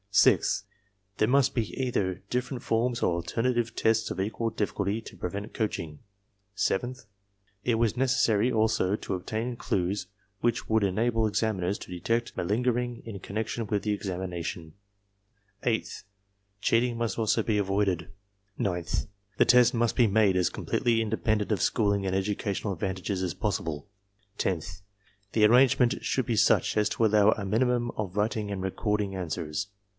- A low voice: Yes, low, 105 Hz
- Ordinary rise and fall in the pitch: Yes, average, 3.4 semitones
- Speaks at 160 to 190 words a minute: No, average, 150 wpm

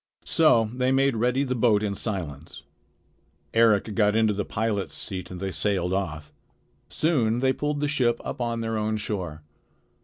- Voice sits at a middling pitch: No, low, 110 Hz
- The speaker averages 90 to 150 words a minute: No, average, 165 wpm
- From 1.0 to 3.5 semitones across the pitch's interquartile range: No, average, 4.1 semitones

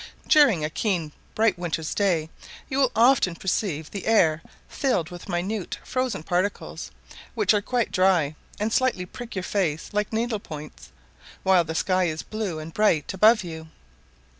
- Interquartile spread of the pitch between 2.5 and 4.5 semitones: No, average, 5.2 semitones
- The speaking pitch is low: No, medium, 185 Hz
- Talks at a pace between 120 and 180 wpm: Yes, average, 160 wpm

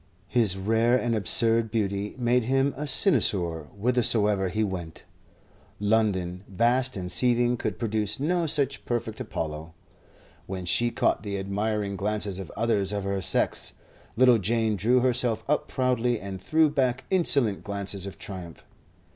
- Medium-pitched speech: No, low, 110 Hz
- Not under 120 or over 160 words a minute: Yes, average, 145 wpm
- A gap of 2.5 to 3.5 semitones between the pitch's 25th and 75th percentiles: No, average, 3.9 semitones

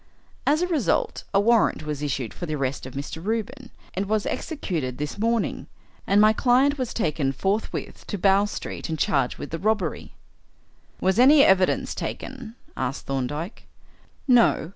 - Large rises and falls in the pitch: Yes, wide, 7.7 semitones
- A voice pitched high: Yes, high, 195 Hz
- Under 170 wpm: Yes, average, 160 wpm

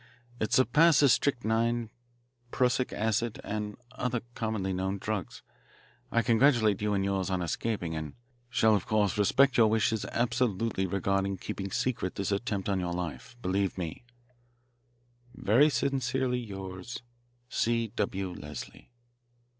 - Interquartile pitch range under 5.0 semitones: Yes, average, 3.7 semitones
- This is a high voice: No, low, 105 Hz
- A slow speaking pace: Yes, slow, 125 wpm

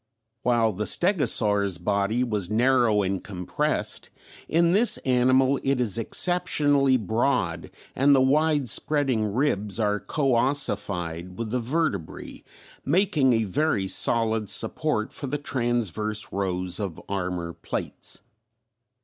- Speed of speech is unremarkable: No, slow, 115 wpm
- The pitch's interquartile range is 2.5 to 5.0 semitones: No, wide, 5.5 semitones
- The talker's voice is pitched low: Yes, low, 115 Hz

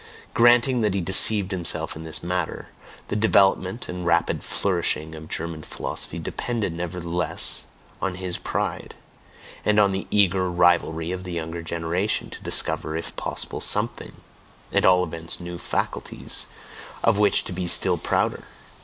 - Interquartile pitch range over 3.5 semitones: No, average, 2.7 semitones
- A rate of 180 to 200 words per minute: No, average, 145 wpm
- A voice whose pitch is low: Yes, very low, 90 Hz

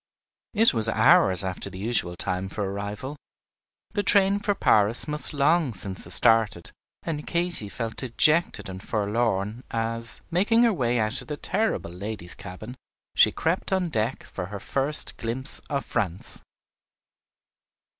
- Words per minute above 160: No, average, 145 wpm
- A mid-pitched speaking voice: No, low, 115 Hz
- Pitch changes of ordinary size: No, wide, 7.0 semitones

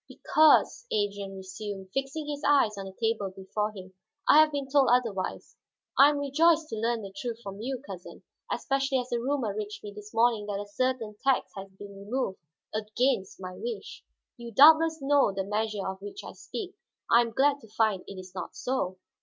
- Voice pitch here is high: Yes, high, 225 Hz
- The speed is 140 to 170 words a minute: No, average, 195 wpm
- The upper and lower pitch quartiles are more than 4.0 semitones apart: Yes, wide, 5.4 semitones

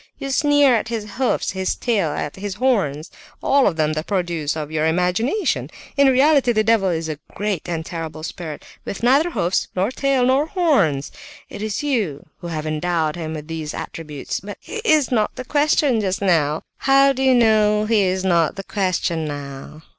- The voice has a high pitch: Yes, high, 195 Hz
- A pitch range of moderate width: No, wide, 8.0 semitones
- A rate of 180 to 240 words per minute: Yes, average, 190 wpm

